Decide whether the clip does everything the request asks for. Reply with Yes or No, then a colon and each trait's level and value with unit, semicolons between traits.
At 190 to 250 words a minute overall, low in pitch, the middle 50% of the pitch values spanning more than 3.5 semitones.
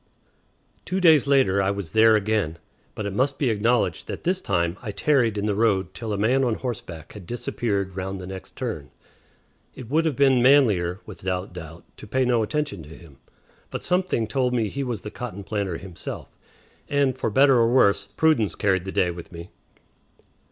Yes: average, 195 wpm; low, 110 Hz; wide, 5.4 semitones